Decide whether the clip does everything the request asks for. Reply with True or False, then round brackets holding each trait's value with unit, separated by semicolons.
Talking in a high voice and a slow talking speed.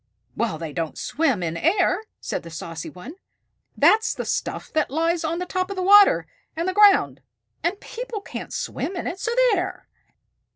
False (340 Hz; 175 wpm)